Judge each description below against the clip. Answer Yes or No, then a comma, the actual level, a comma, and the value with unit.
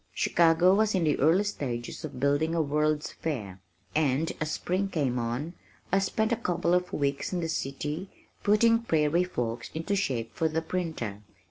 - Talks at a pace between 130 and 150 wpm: No, average, 170 wpm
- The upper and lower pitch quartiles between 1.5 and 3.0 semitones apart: No, average, 4.7 semitones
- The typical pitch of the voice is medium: Yes, medium, 160 Hz